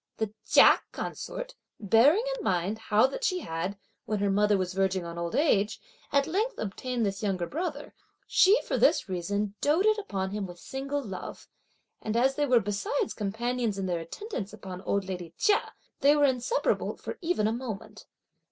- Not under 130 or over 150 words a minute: No, average, 175 wpm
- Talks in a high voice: Yes, high, 215 Hz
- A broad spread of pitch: Yes, wide, 6.8 semitones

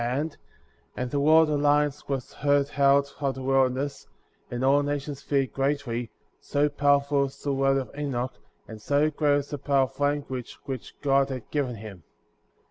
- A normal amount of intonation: No, narrow, 1.5 semitones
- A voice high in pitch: No, medium, 140 Hz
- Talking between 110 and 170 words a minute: No, average, 185 wpm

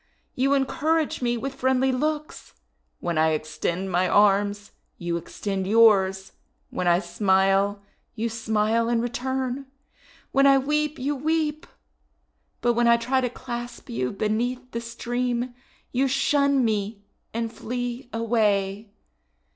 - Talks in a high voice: Yes, high, 235 Hz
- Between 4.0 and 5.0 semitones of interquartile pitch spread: Yes, average, 4.4 semitones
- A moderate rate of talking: No, slow, 130 wpm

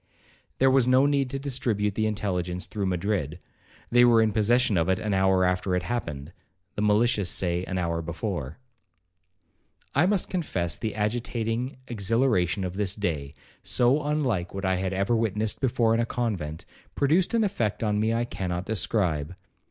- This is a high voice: No, low, 105 Hz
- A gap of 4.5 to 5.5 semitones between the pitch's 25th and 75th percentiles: Yes, average, 4.8 semitones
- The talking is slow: No, average, 160 wpm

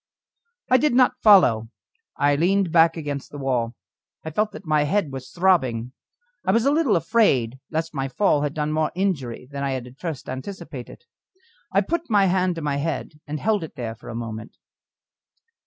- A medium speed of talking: Yes, average, 190 wpm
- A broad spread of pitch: Yes, wide, 6.5 semitones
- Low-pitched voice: No, medium, 155 Hz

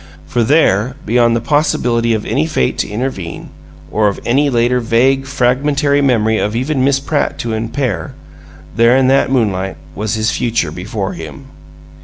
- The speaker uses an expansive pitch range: No, average, 3.7 semitones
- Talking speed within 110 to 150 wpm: No, average, 160 wpm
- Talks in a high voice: No, low, 120 Hz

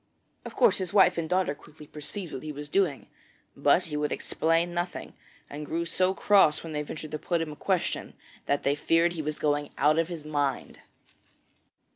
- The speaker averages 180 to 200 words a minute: Yes, average, 195 wpm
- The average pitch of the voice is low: No, medium, 160 Hz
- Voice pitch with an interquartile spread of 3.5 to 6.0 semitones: No, average, 2.7 semitones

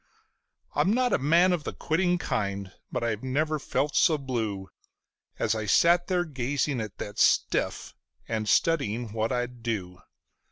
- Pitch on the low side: Yes, low, 125 Hz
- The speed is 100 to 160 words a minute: Yes, average, 155 wpm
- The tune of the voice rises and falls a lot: Yes, wide, 6.6 semitones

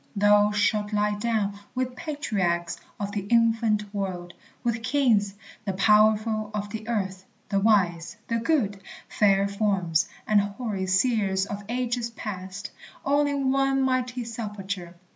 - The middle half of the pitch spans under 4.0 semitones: Yes, average, 2.9 semitones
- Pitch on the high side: Yes, high, 210 Hz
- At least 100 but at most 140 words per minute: Yes, slow, 135 wpm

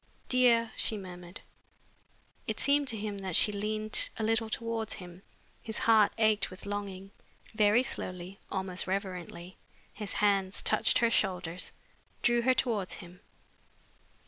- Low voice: No, high, 205 Hz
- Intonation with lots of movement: No, average, 3.2 semitones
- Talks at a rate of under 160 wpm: Yes, slow, 135 wpm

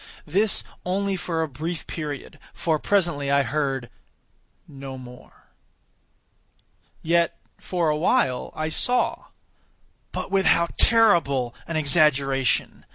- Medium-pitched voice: Yes, medium, 155 Hz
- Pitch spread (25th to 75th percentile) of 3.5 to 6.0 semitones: Yes, average, 4.0 semitones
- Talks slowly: Yes, slow, 105 wpm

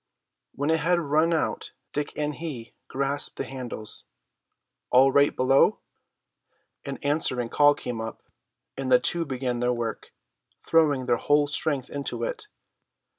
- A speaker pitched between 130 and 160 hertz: Yes, medium, 140 Hz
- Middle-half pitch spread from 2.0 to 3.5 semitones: Yes, average, 3.0 semitones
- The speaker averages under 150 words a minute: Yes, average, 140 wpm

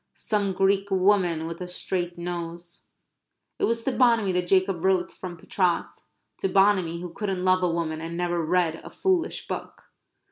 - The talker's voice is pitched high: No, medium, 180 Hz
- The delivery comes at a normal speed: Yes, average, 170 wpm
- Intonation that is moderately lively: No, narrow, 2.2 semitones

